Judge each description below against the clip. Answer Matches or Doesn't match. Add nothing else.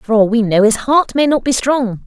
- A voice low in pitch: Doesn't match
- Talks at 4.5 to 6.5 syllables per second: Matches